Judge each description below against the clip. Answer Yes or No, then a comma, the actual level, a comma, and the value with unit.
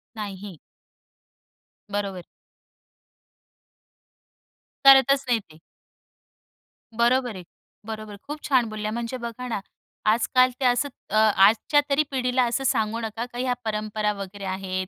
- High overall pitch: Yes, high, 225 Hz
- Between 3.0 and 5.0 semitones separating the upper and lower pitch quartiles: Yes, average, 3.4 semitones